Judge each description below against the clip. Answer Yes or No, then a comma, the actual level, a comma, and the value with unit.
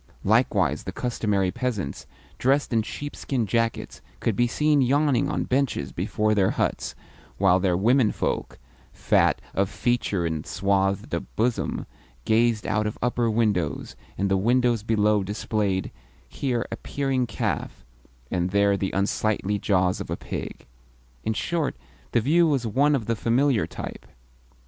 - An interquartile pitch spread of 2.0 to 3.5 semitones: No, average, 4.2 semitones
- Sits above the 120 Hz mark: No, low, 110 Hz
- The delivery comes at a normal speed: Yes, average, 145 wpm